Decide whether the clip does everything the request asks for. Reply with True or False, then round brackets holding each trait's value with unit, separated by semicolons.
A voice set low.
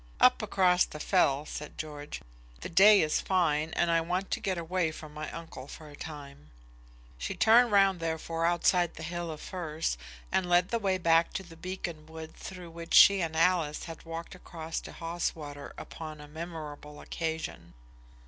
False (165 Hz)